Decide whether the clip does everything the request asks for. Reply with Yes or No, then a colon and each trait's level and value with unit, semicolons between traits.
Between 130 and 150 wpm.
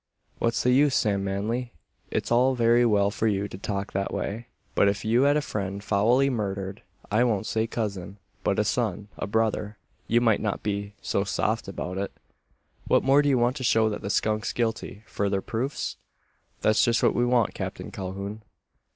No: average, 190 wpm